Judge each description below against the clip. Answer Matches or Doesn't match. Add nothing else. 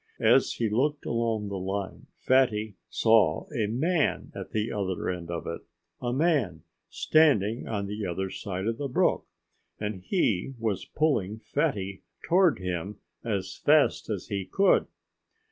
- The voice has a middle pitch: Doesn't match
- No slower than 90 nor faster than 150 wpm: Matches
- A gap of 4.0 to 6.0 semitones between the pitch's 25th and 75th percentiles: Matches